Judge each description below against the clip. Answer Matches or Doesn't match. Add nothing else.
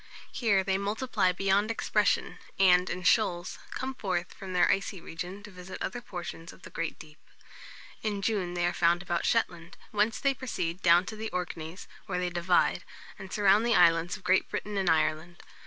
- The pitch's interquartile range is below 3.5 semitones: Matches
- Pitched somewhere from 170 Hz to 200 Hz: Matches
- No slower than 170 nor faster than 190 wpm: Matches